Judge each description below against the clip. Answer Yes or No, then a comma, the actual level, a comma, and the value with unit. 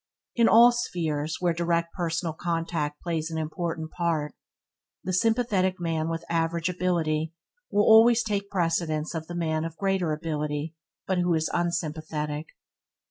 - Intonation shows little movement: Yes, narrow, 2.3 semitones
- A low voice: No, medium, 170 Hz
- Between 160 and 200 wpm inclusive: No, average, 140 wpm